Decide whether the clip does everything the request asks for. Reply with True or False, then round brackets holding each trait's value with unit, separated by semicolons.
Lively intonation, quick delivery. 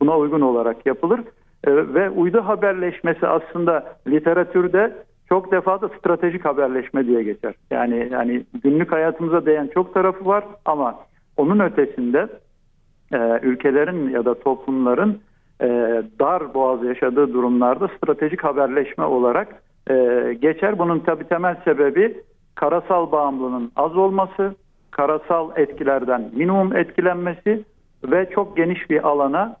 False (5.8 semitones; 120 wpm)